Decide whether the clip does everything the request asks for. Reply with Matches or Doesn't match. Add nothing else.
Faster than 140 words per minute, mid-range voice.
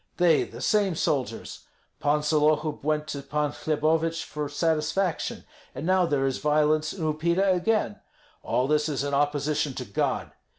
Matches